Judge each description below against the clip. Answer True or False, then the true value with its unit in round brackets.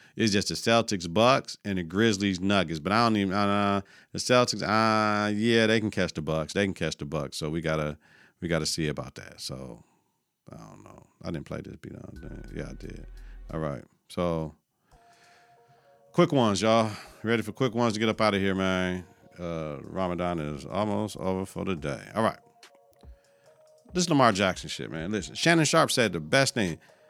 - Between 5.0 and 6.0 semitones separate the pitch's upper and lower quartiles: True (5.3 semitones)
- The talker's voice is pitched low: True (100 Hz)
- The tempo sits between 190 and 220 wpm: True (200 wpm)